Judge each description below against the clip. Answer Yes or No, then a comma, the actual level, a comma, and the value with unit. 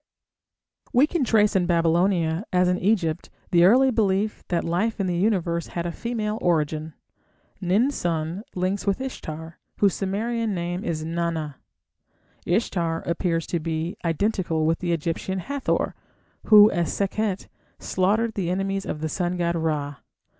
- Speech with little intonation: No, average, 3.7 semitones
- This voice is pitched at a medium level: Yes, medium, 180 Hz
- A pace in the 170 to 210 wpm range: No, average, 145 wpm